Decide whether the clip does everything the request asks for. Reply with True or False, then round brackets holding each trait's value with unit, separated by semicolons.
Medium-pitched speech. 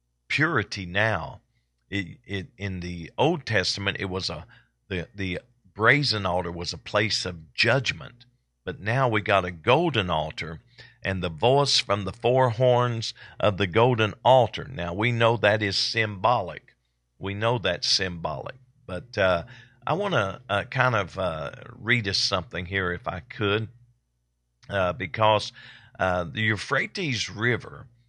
False (105 Hz)